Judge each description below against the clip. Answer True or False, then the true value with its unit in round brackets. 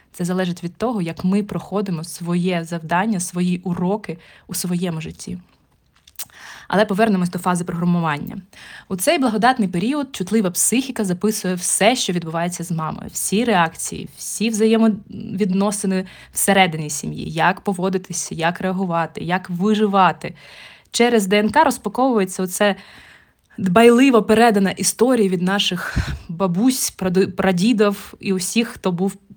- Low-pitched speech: False (190 Hz)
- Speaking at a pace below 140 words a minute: True (120 wpm)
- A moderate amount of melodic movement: True (3.2 semitones)